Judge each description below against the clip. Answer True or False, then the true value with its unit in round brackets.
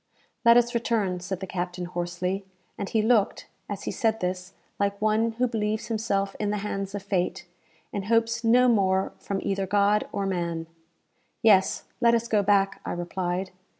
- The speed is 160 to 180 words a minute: True (175 wpm)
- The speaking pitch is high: True (200 Hz)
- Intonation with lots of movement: False (2.9 semitones)